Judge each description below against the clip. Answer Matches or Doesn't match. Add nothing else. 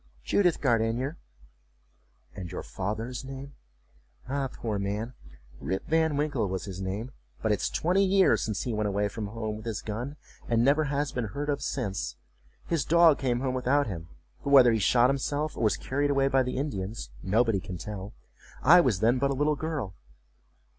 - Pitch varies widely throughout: Matches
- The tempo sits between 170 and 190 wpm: Matches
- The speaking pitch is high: Doesn't match